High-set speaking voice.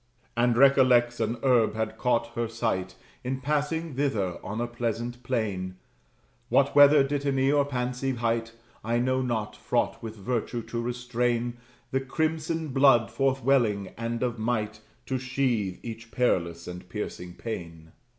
No: low, 120 Hz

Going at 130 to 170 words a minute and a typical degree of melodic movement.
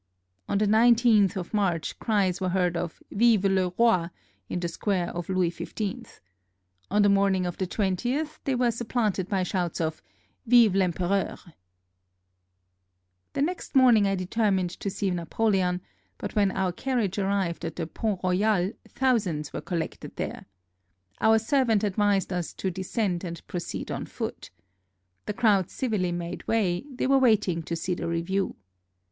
Yes: average, 165 wpm; average, 3.7 semitones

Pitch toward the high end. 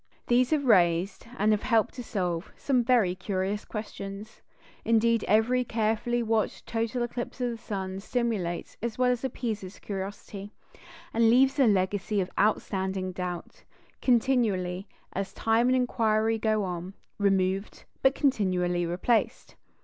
Yes: high, 215 Hz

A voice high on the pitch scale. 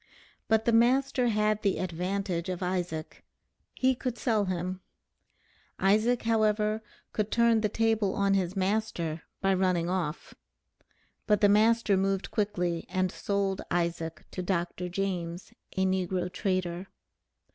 Yes: high, 195 Hz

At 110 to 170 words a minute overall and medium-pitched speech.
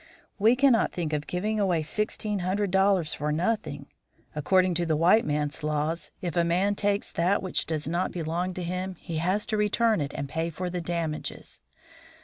No: average, 190 wpm; medium, 180 Hz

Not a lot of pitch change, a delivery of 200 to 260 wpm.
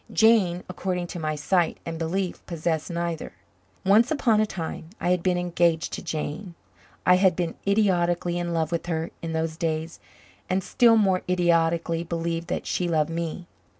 No: narrow, 1.9 semitones; average, 170 wpm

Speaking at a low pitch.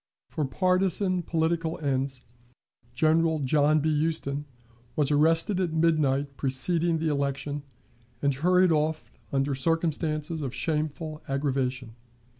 No: medium, 155 Hz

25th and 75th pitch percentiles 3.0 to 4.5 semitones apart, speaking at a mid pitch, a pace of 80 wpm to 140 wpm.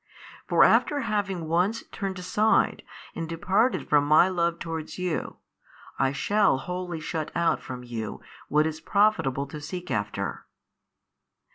Yes: average, 4.0 semitones; medium, 170 Hz; slow, 135 wpm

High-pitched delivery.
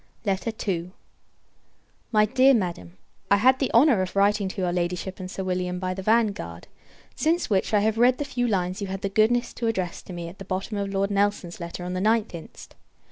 Yes: high, 195 Hz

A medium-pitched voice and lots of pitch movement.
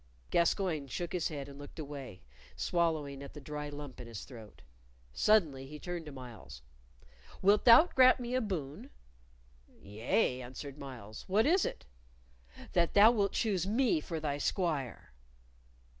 Yes: medium, 150 Hz; wide, 6.5 semitones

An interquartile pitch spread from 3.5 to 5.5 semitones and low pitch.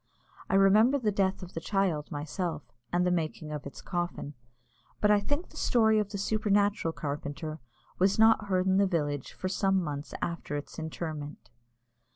No: average, 4.6 semitones; medium, 185 Hz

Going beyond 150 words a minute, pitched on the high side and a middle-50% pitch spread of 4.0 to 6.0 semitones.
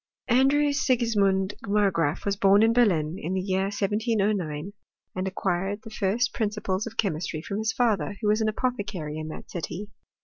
No: average, 165 wpm; high, 200 Hz; average, 3.0 semitones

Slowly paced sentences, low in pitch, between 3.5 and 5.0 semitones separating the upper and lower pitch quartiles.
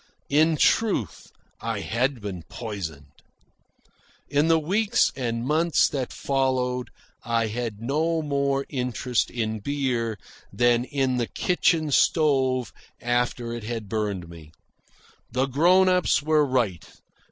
Yes: slow, 120 wpm; low, 125 Hz; average, 4.2 semitones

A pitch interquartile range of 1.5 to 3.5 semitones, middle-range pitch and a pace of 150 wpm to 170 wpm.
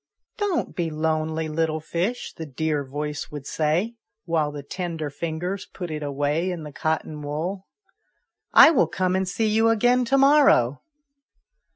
No: average, 4.1 semitones; medium, 160 Hz; average, 160 wpm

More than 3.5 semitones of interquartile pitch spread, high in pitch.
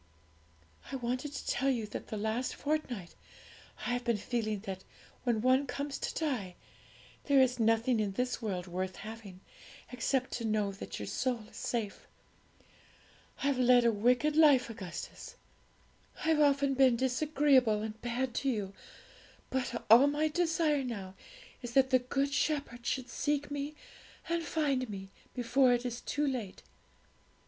Yes: average, 4.0 semitones; very high, 250 Hz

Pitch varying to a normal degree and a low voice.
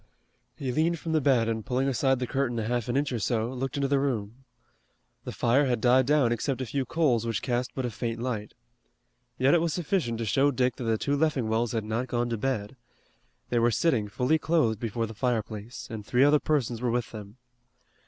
Yes: average, 3.1 semitones; low, 125 Hz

